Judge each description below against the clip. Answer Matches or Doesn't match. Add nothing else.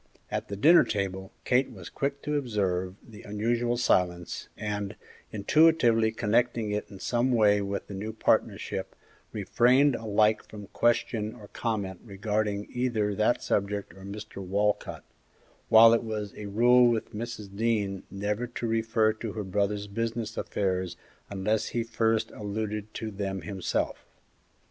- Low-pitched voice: Matches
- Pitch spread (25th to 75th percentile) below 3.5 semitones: Matches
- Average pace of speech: Matches